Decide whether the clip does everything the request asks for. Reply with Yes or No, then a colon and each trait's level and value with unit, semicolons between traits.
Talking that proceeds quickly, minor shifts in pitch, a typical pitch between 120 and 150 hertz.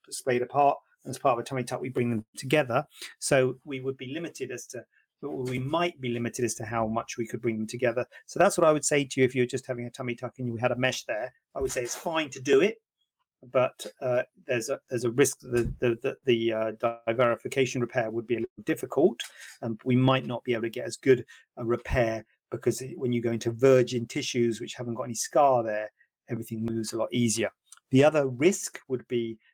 Yes: fast, 240 wpm; narrow, 2.1 semitones; low, 125 Hz